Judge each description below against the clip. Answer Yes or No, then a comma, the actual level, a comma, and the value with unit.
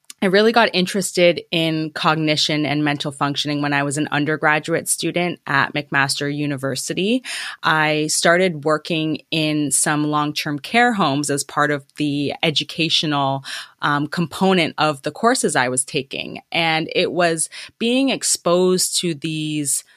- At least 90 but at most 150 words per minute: Yes, average, 140 wpm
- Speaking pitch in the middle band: Yes, medium, 155 Hz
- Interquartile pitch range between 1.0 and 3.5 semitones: Yes, average, 3.1 semitones